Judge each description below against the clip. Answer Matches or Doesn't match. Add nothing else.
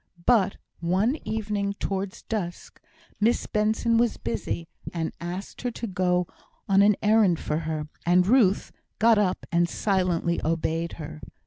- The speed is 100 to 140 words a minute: Matches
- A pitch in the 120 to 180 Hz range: Doesn't match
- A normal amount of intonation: Matches